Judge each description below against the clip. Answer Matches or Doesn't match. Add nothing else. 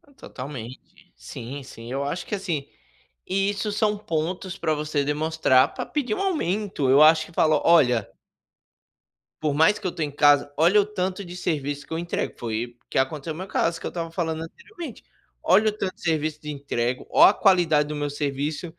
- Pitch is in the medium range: Matches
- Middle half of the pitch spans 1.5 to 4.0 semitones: Doesn't match